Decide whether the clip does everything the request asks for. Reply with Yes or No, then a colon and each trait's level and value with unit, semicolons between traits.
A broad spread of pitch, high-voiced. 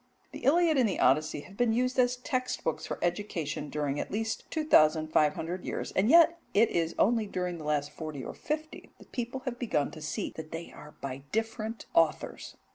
Yes: wide, 8.0 semitones; high, 195 Hz